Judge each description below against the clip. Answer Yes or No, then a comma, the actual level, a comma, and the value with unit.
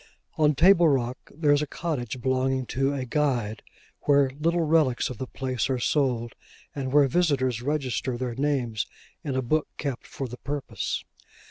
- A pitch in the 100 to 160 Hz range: Yes, low, 135 Hz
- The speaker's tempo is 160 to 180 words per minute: Yes, average, 165 wpm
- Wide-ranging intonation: No, average, 2.8 semitones